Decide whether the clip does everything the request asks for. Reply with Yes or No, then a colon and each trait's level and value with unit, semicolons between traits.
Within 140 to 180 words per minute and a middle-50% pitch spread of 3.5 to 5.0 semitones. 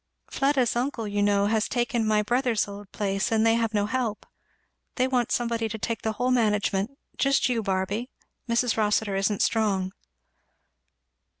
No: average, 160 wpm; average, 2.8 semitones